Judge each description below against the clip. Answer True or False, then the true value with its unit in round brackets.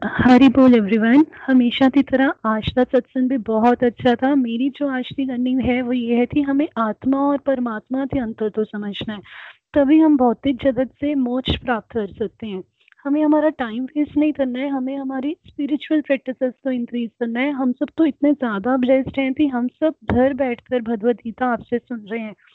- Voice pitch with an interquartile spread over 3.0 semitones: False (2.7 semitones)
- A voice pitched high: True (260 Hz)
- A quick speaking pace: True (195 wpm)